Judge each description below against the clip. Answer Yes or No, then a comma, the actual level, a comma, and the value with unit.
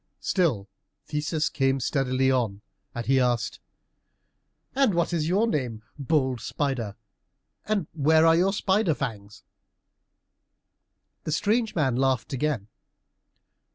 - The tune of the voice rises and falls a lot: No, average, 5.0 semitones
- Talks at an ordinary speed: No, slow, 115 wpm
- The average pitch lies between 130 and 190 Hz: Yes, medium, 140 Hz